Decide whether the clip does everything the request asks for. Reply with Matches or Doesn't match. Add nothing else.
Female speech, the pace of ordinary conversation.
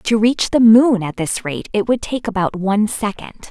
Doesn't match